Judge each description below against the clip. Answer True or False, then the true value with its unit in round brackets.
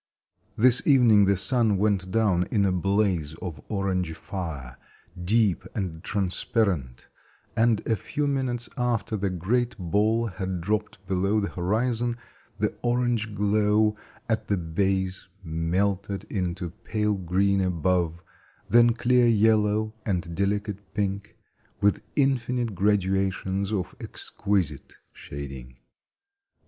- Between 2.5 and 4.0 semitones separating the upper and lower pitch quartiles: True (3.3 semitones)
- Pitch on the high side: False (100 Hz)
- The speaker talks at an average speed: False (115 wpm)